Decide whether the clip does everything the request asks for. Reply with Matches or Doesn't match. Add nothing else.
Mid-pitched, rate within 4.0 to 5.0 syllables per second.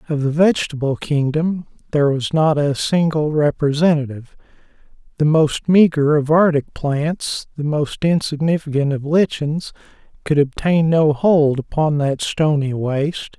Matches